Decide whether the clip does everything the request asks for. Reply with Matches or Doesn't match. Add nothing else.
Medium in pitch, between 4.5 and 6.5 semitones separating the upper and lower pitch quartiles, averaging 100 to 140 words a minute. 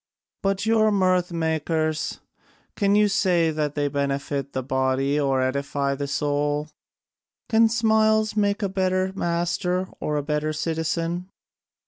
Matches